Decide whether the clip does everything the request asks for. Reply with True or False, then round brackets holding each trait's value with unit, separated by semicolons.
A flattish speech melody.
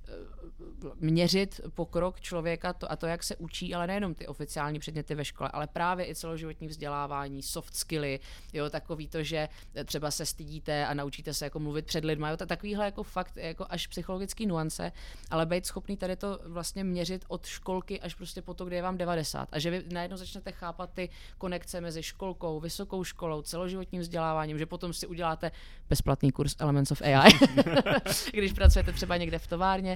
False (3.1 semitones)